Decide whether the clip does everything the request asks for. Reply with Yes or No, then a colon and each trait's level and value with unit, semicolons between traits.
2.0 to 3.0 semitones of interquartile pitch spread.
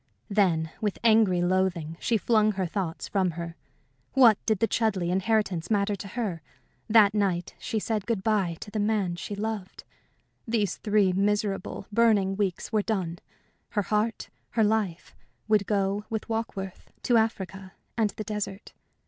Yes: narrow, 2.6 semitones